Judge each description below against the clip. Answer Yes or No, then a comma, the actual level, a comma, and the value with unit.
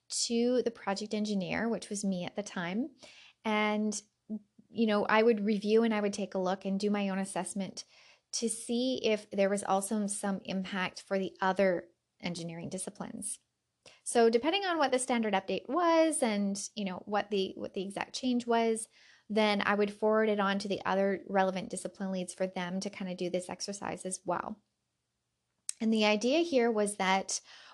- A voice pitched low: No, high, 205 Hz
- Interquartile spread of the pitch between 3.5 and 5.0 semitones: No, average, 2.8 semitones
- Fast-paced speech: No, average, 185 wpm